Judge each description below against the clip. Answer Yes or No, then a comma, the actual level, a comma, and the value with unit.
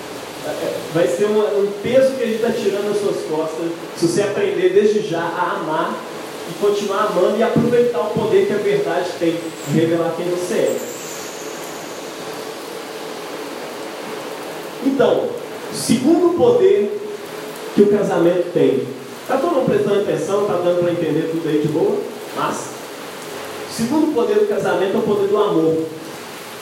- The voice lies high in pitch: Yes, high, 210 Hz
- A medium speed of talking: Yes, average, 150 wpm